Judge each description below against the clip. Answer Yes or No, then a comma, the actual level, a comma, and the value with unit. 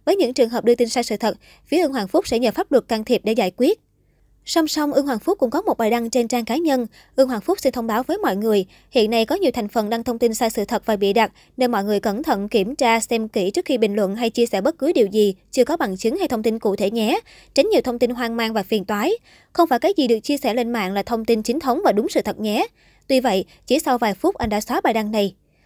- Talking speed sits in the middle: No, fast, 305 wpm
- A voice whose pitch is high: Yes, high, 235 Hz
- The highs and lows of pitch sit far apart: No, average, 3.4 semitones